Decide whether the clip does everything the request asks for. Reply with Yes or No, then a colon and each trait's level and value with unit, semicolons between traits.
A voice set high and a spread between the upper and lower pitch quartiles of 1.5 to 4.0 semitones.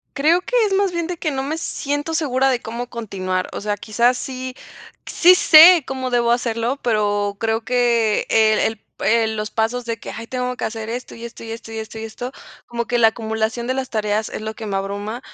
Yes: high, 235 Hz; average, 2.8 semitones